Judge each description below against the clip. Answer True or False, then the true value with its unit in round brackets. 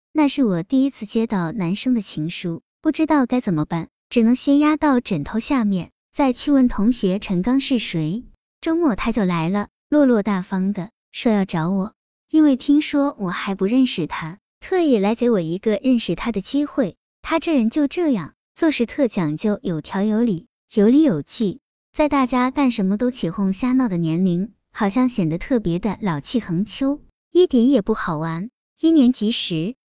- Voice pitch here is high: True (225 Hz)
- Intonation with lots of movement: True (6.2 semitones)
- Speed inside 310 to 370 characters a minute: False (260 characters per minute)